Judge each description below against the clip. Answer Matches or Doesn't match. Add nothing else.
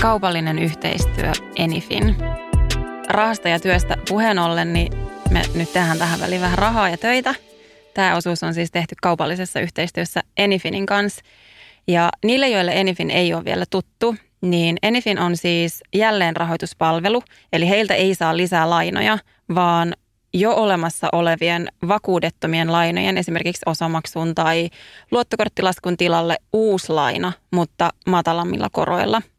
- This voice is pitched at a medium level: Matches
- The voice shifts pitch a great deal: Doesn't match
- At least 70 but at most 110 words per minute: Doesn't match